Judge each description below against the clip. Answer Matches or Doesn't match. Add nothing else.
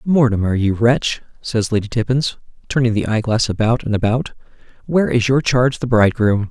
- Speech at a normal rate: Matches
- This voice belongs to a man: Matches